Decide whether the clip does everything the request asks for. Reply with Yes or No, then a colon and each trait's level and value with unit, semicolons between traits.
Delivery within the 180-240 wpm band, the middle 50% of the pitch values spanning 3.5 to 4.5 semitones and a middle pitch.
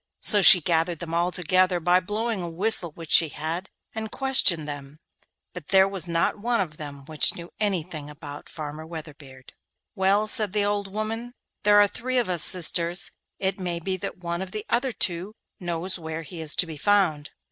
Yes: average, 190 wpm; average, 4.1 semitones; medium, 180 Hz